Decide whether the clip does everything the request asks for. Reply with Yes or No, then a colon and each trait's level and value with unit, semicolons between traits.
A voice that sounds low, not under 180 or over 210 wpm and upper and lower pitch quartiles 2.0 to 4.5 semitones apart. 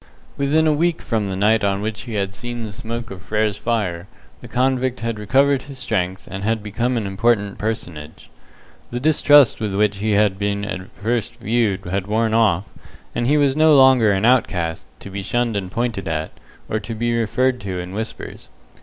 Yes: low, 110 Hz; average, 195 wpm; average, 3.6 semitones